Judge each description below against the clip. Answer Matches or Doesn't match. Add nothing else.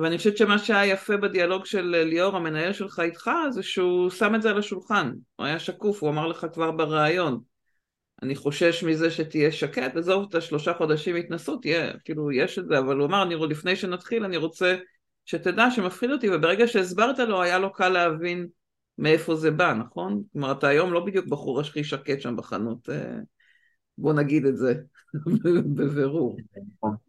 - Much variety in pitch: Doesn't match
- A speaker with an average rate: Doesn't match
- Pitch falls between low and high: Matches